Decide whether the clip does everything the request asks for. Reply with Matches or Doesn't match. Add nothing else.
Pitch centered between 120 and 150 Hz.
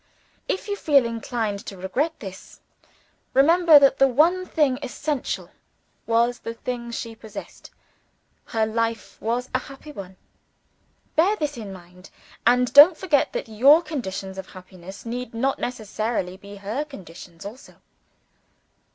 Doesn't match